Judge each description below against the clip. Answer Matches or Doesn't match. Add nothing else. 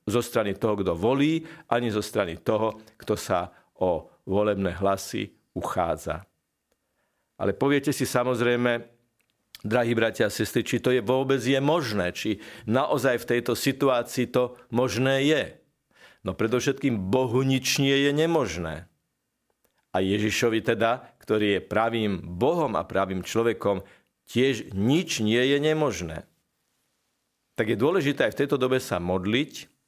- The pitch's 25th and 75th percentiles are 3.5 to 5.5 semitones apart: Matches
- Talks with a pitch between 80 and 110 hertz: Doesn't match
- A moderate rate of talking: Matches